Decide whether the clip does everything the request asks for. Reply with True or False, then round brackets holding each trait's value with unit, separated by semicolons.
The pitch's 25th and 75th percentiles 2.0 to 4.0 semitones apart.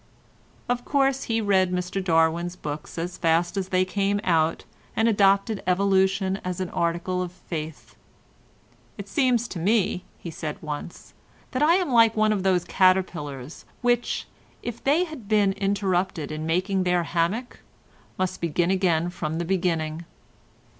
True (3.3 semitones)